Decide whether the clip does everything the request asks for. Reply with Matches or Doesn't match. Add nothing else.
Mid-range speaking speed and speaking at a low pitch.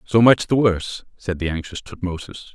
Matches